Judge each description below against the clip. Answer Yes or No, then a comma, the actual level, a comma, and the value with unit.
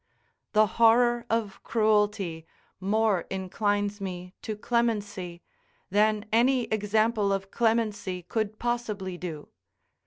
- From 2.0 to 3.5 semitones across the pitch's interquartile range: Yes, average, 2.8 semitones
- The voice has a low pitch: No, high, 210 Hz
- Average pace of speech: No, slow, 100 wpm